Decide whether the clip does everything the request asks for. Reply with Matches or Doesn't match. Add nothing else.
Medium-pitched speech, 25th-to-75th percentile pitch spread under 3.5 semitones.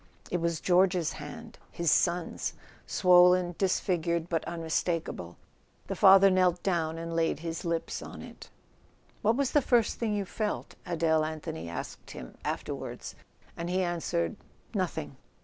Matches